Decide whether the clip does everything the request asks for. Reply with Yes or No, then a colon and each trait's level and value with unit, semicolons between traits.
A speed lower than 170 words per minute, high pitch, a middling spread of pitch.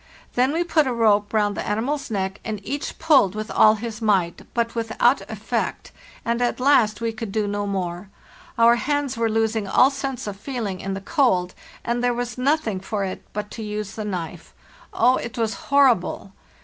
No: average, 190 wpm; high, 225 Hz; average, 3.4 semitones